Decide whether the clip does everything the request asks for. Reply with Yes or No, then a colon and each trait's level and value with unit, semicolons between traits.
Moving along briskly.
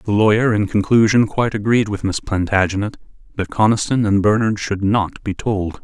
No: average, 175 wpm